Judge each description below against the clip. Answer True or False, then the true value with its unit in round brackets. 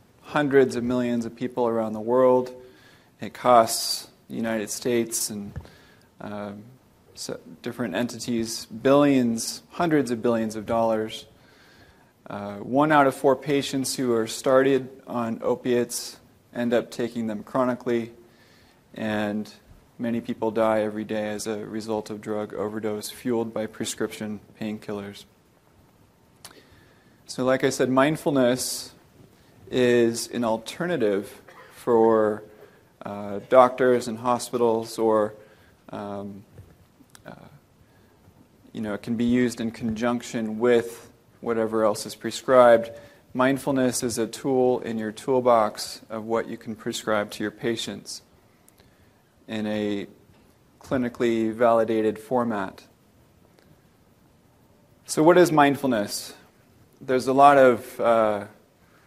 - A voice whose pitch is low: True (115 Hz)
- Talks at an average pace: False (115 wpm)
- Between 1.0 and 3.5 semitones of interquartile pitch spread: True (2.6 semitones)